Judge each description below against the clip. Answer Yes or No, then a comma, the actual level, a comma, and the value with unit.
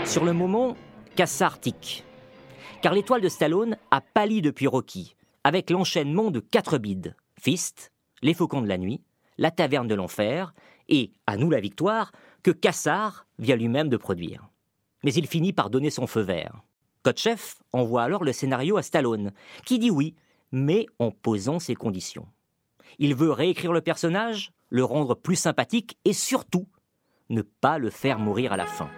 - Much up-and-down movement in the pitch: Yes, wide, 7.3 semitones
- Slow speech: No, average, 165 wpm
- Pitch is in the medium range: Yes, medium, 155 Hz